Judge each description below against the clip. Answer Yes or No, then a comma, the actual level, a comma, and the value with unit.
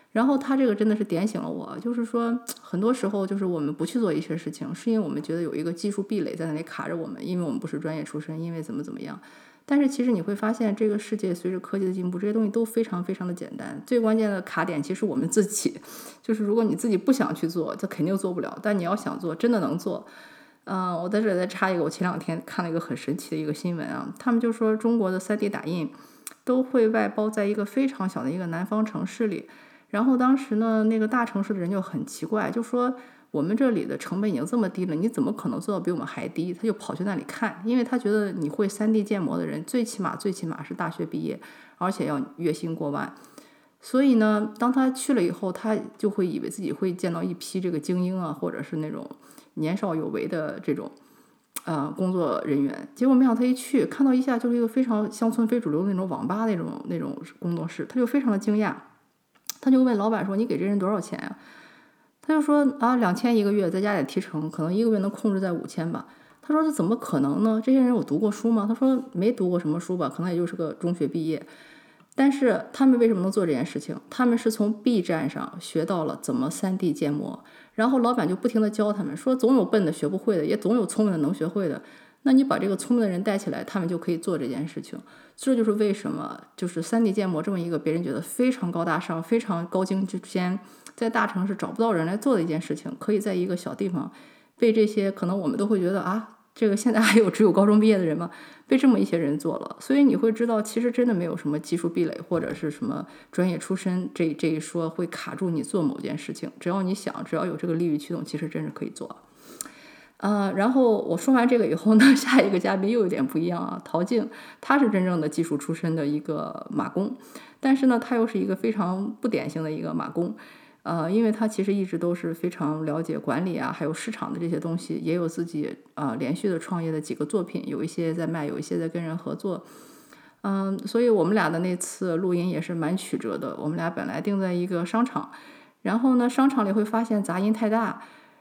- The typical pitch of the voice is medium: No, high, 210 Hz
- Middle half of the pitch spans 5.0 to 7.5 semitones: Yes, wide, 5.5 semitones